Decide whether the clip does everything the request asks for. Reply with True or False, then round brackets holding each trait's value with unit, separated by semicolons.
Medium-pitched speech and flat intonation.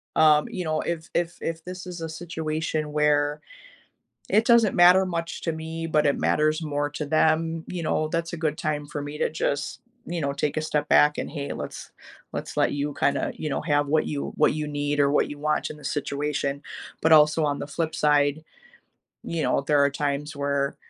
True (150 Hz; 1.8 semitones)